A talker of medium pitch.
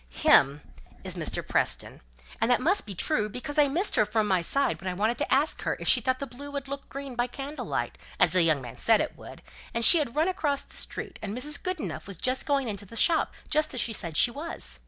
No: very high, 250 Hz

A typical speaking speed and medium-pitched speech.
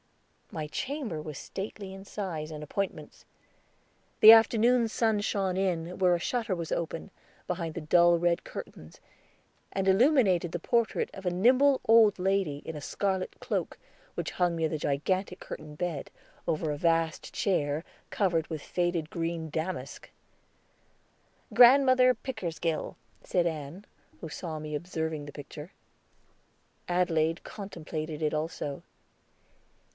No: slow, 130 wpm; medium, 175 Hz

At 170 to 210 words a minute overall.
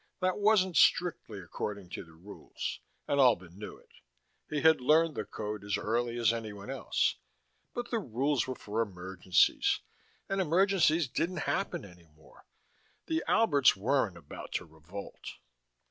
No: average, 145 wpm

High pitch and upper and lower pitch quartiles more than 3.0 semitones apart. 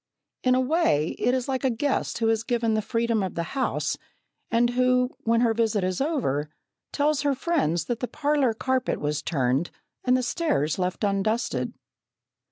Yes: high, 235 Hz; average, 5.2 semitones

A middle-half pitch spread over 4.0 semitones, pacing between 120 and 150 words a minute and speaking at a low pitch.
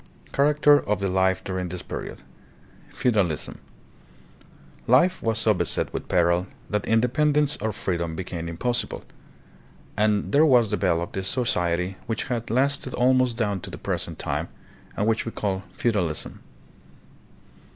Yes: average, 5.1 semitones; average, 140 wpm; low, 105 Hz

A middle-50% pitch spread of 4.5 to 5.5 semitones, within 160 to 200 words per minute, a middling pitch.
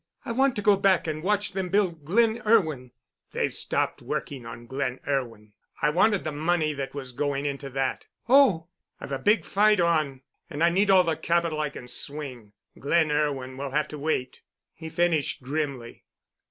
Yes: average, 5.1 semitones; average, 180 wpm; medium, 155 Hz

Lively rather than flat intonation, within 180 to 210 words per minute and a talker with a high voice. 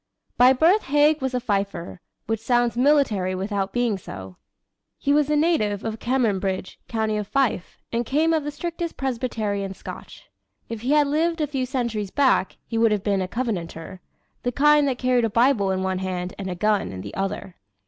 Yes: wide, 5.9 semitones; average, 190 wpm; high, 230 Hz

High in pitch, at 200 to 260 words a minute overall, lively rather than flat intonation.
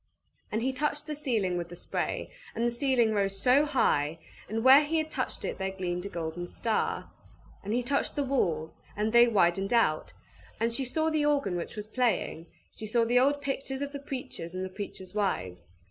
Yes: high, 230 Hz; fast, 205 wpm; wide, 6.4 semitones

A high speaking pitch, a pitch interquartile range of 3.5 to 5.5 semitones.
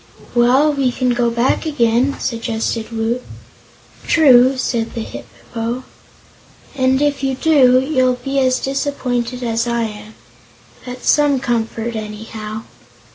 No: high, 245 Hz; narrow, 2.6 semitones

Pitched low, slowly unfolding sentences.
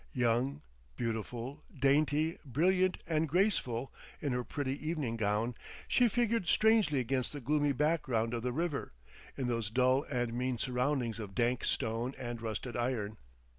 No: low, 130 Hz; average, 145 wpm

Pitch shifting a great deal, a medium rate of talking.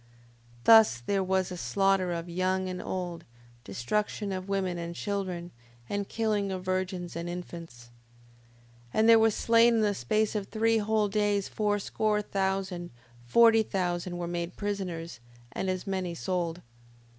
No: average, 2.8 semitones; average, 155 wpm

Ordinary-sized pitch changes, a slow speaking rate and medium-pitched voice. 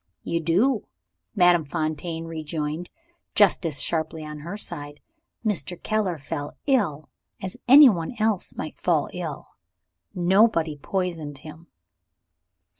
Yes: average, 4.0 semitones; slow, 115 wpm; medium, 170 Hz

